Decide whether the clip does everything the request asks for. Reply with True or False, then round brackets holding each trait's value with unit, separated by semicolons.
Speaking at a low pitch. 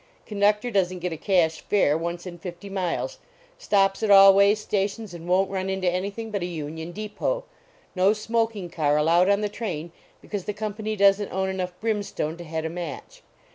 False (190 Hz)